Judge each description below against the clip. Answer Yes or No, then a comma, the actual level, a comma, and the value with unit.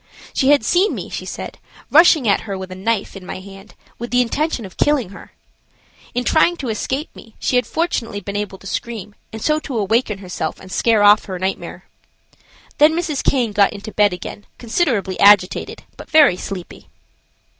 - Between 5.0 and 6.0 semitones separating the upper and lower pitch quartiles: Yes, wide, 5.4 semitones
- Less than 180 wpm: No, average, 190 wpm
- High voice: Yes, high, 220 Hz